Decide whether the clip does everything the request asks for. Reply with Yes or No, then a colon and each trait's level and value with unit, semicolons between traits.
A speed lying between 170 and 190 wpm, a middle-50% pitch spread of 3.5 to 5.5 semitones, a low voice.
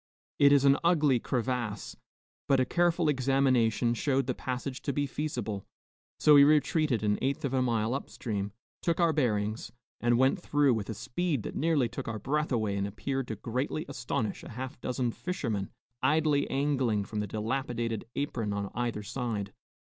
Yes: average, 175 wpm; average, 4.1 semitones; low, 130 Hz